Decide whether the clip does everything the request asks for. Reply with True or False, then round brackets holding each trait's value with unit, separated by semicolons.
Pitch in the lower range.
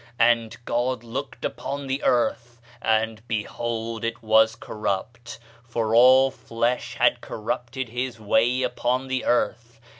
True (120 Hz)